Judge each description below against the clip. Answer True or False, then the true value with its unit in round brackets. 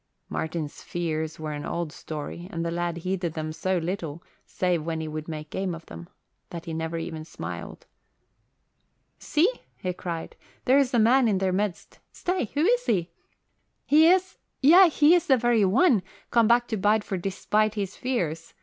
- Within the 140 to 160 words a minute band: False (175 wpm)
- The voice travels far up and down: True (6.6 semitones)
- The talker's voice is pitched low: False (185 Hz)